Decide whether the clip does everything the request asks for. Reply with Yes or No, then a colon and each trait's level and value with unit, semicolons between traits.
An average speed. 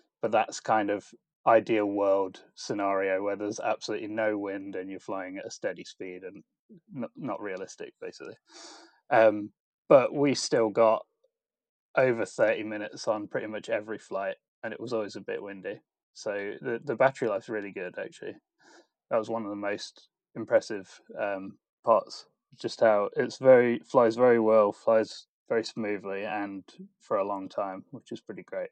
Yes: average, 165 wpm